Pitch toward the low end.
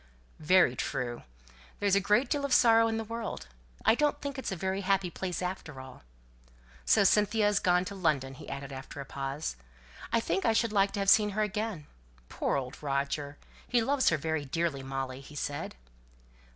No: medium, 185 Hz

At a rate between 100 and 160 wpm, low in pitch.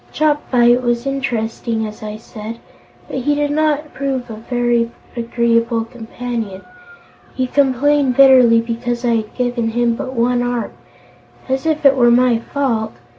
No: average, 145 wpm; high, 245 Hz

